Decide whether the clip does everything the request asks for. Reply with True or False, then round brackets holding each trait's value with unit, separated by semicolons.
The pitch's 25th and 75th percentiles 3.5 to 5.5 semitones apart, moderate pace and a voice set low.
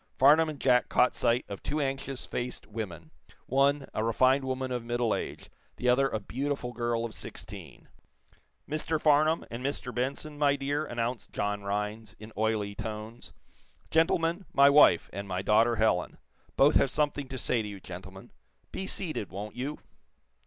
True (4.6 semitones; 165 wpm; 125 Hz)